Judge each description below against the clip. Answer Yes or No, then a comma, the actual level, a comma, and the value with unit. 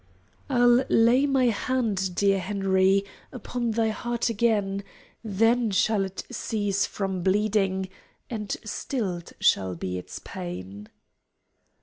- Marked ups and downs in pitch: No, average, 3.5 semitones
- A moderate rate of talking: No, slow, 110 wpm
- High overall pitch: Yes, high, 205 Hz